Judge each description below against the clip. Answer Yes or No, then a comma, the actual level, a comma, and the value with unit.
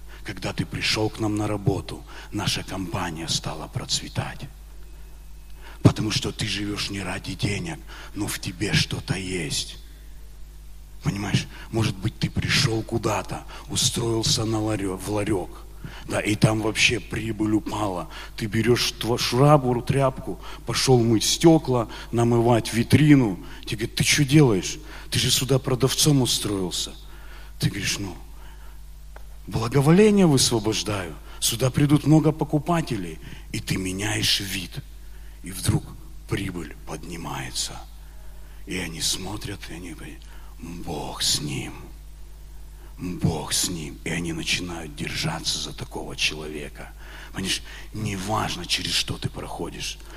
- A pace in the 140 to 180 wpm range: No, average, 120 wpm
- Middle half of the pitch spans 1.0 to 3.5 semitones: No, average, 4.8 semitones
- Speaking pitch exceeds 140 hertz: No, low, 115 Hz